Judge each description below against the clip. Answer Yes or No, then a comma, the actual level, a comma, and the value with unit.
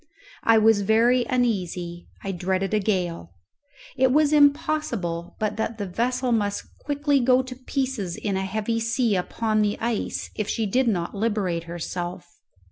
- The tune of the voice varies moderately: Yes, average, 4.8 semitones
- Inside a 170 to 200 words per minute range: No, average, 155 wpm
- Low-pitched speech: No, high, 215 Hz